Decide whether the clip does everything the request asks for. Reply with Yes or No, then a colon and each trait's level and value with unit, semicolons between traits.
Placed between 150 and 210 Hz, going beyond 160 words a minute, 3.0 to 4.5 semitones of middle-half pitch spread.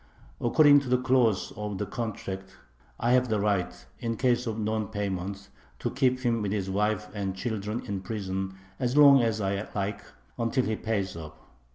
No: low, 105 Hz; average, 180 wpm; average, 3.5 semitones